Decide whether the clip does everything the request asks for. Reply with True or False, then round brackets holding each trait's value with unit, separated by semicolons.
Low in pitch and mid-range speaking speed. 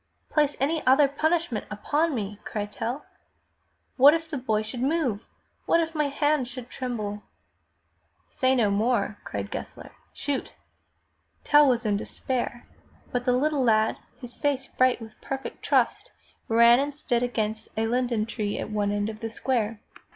False (245 Hz; 160 wpm)